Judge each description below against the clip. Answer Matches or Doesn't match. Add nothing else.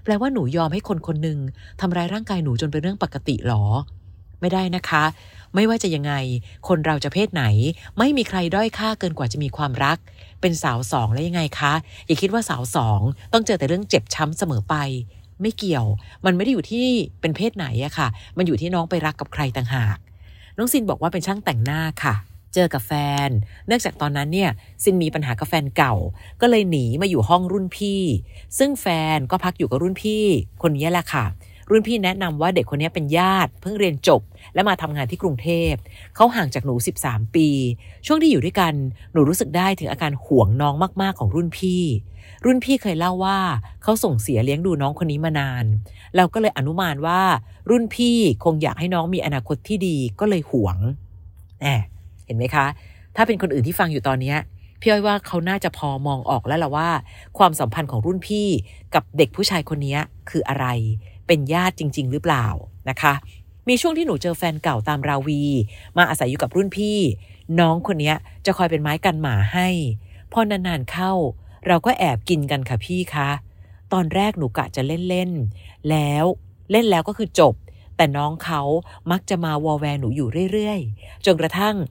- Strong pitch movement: Matches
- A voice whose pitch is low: Doesn't match